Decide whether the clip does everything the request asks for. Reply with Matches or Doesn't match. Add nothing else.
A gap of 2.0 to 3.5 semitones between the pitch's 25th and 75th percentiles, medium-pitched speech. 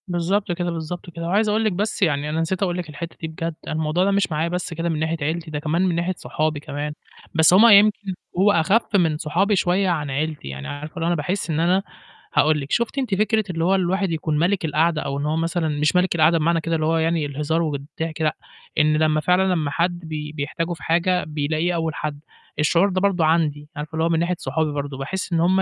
Matches